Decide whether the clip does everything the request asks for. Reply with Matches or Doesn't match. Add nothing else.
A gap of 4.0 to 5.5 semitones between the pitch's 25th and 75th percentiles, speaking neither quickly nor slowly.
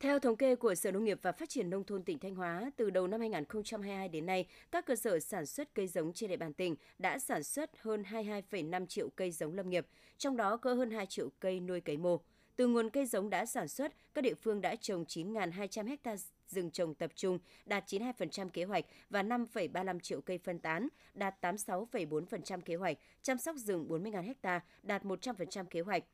Matches